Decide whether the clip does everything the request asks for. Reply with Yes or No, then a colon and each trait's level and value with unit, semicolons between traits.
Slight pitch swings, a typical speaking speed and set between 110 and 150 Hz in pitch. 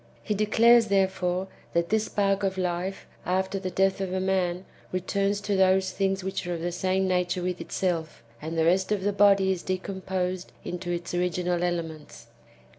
No: narrow, 1.6 semitones; average, 180 wpm; medium, 185 Hz